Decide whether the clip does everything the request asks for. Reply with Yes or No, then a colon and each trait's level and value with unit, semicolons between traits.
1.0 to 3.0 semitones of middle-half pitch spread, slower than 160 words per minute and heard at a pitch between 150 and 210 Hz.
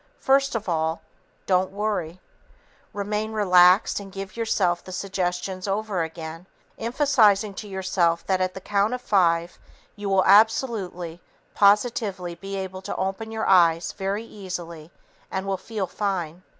Yes: average, 2.7 semitones; average, 140 wpm; high, 190 Hz